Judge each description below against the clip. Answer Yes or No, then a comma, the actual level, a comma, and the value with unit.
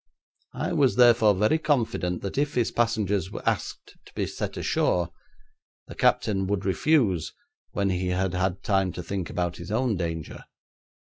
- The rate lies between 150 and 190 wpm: Yes, average, 155 wpm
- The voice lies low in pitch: Yes, low, 100 Hz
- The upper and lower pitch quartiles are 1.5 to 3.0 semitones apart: No, average, 4.3 semitones